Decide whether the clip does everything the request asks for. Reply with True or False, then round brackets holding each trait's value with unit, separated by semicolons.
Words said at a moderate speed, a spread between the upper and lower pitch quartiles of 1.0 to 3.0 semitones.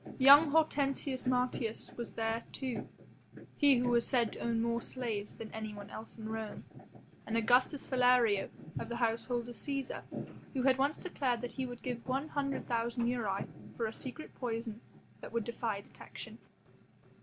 True (165 wpm; 2.5 semitones)